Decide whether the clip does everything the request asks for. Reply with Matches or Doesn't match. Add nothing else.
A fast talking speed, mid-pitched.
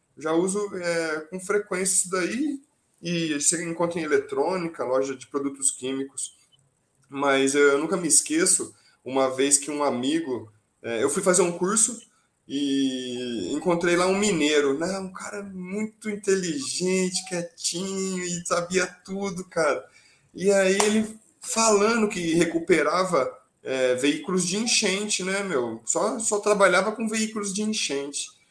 Doesn't match